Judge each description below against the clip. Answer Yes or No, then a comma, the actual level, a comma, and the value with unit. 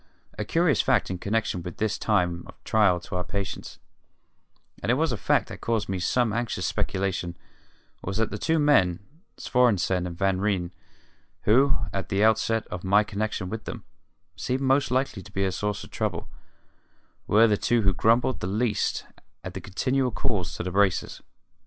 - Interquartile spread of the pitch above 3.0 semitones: Yes, average, 4.1 semitones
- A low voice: Yes, low, 105 Hz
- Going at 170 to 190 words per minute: Yes, average, 175 wpm